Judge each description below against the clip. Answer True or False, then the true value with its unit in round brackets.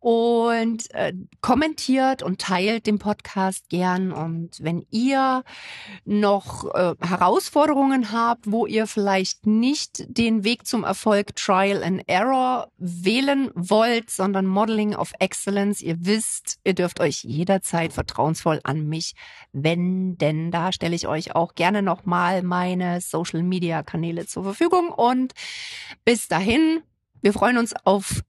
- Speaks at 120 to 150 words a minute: True (135 wpm)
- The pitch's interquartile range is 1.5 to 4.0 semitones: False (4.7 semitones)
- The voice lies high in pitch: True (195 Hz)